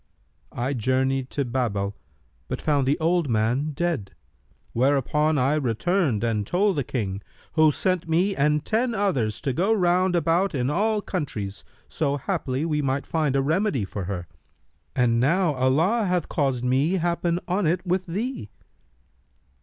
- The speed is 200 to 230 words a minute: No, average, 155 wpm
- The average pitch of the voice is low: No, medium, 150 Hz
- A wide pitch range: Yes, wide, 5.8 semitones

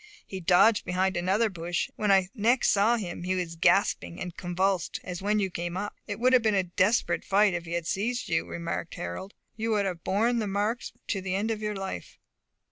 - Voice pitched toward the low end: No, high, 195 Hz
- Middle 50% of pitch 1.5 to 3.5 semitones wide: Yes, average, 3.1 semitones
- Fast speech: Yes, fast, 220 wpm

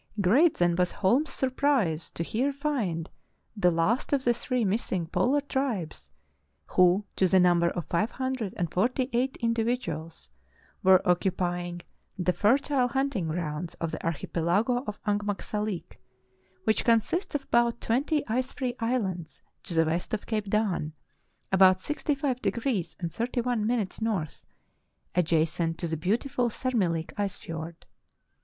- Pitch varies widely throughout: Yes, wide, 6.2 semitones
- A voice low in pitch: No, high, 205 Hz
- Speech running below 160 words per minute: Yes, slow, 135 wpm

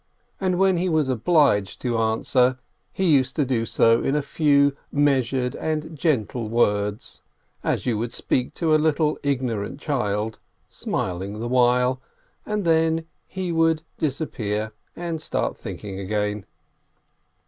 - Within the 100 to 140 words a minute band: Yes, slow, 135 wpm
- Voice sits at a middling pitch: No, low, 130 Hz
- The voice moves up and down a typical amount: No, wide, 5.9 semitones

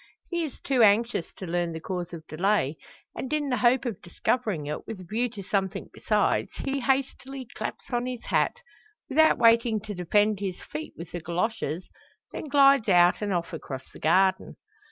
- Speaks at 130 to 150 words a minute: No, average, 185 wpm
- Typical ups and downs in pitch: No, wide, 6.0 semitones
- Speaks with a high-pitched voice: Yes, high, 210 Hz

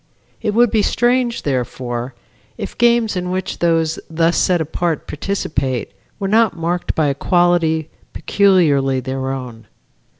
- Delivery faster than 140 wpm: No, slow, 135 wpm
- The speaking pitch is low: No, medium, 170 Hz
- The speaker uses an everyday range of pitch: No, wide, 6.6 semitones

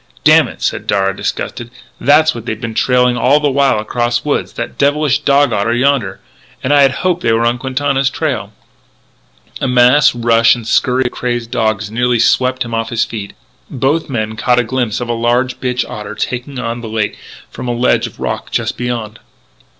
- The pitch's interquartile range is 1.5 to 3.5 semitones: Yes, narrow, 2.4 semitones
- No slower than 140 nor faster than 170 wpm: No, fast, 205 wpm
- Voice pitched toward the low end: Yes, low, 120 Hz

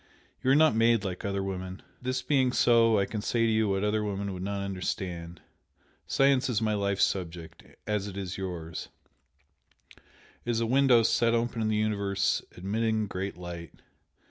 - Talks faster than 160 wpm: Yes, average, 175 wpm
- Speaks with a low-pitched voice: Yes, low, 105 Hz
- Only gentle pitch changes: No, average, 3.3 semitones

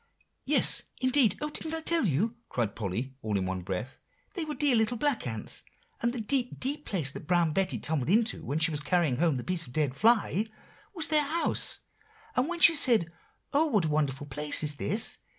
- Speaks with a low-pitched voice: No, medium, 180 Hz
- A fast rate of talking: Yes, fast, 210 wpm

